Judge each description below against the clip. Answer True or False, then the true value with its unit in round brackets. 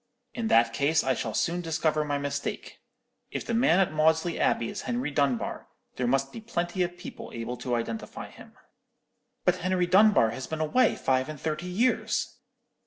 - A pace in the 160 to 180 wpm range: True (175 wpm)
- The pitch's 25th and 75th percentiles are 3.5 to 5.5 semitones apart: True (5.2 semitones)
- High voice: False (155 Hz)